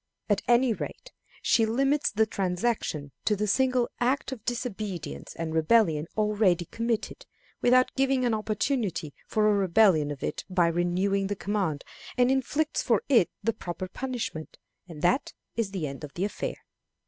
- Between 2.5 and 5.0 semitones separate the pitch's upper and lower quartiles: No, wide, 5.6 semitones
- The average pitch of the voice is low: No, high, 210 Hz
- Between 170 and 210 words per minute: No, average, 160 wpm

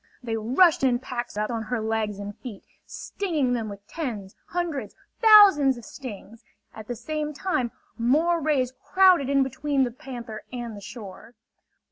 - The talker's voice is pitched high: Yes, high, 245 Hz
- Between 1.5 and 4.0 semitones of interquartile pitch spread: No, average, 5.1 semitones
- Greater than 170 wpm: No, average, 155 wpm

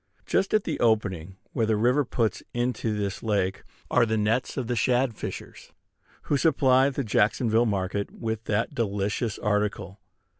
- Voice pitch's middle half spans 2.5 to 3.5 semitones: Yes, average, 3.1 semitones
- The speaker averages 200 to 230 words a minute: No, average, 155 wpm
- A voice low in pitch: Yes, low, 110 Hz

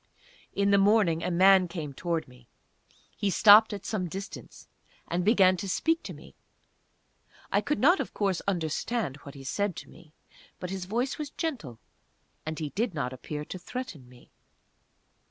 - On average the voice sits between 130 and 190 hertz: Yes, medium, 185 Hz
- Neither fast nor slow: Yes, average, 170 wpm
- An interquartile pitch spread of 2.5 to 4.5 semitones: No, average, 5.1 semitones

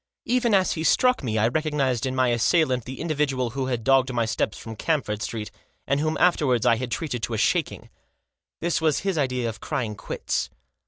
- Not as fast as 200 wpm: No, fast, 205 wpm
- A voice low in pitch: Yes, low, 130 Hz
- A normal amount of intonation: Yes, average, 5.0 semitones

